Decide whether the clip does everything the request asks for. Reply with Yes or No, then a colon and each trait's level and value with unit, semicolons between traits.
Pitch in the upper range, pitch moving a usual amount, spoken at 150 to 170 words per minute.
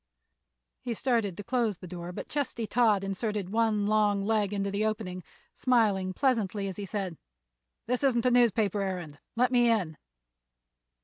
Yes: high, 210 Hz; average, 3.3 semitones; average, 160 wpm